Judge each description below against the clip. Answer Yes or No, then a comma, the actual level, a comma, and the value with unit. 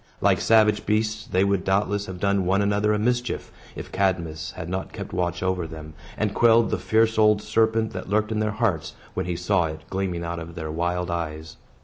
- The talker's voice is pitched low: Yes, very low, 95 Hz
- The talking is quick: Yes, fast, 210 wpm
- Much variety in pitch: No, average, 3.7 semitones